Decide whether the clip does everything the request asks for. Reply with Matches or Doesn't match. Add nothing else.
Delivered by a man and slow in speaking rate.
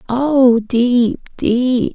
Doesn't match